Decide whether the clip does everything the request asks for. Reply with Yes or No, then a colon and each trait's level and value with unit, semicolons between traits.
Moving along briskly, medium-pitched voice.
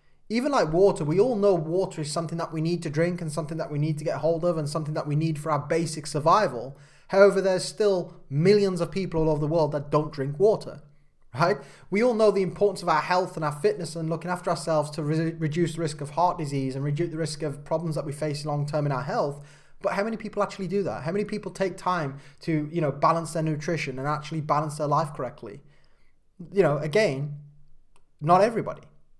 Yes: fast, 230 wpm; medium, 160 Hz